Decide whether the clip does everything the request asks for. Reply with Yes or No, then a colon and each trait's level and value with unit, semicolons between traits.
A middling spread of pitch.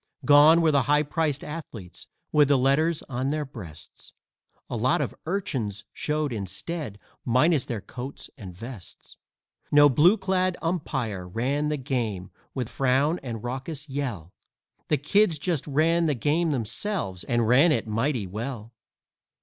Yes: average, 5.0 semitones